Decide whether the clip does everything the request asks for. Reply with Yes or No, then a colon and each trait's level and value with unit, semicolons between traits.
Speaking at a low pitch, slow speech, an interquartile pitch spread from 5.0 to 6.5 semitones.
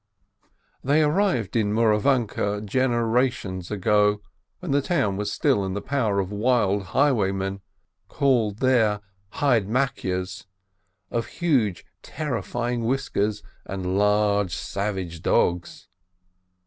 No: low, 105 Hz; slow, 100 wpm; average, 4.4 semitones